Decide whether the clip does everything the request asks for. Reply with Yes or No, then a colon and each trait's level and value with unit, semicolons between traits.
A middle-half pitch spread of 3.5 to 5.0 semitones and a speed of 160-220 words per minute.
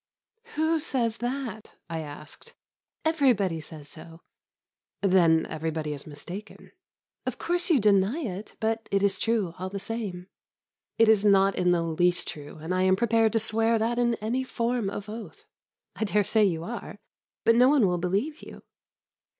Yes: average, 4.6 semitones; average, 165 wpm